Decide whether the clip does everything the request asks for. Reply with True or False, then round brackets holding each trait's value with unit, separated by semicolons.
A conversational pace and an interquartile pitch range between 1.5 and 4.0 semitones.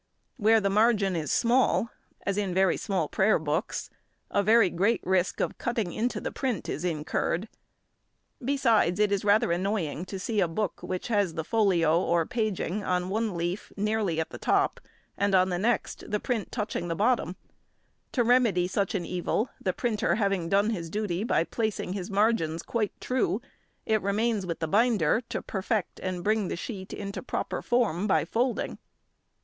True (175 wpm; 3.7 semitones)